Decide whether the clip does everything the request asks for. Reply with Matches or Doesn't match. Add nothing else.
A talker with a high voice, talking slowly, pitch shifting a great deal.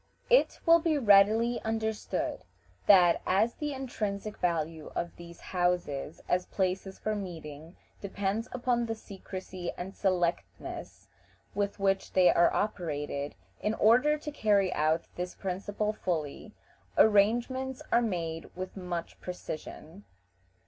Doesn't match